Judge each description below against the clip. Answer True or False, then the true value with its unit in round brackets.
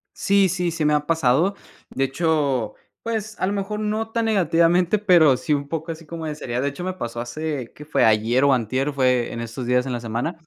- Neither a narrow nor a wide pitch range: False (5.8 semitones)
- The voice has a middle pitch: True (150 Hz)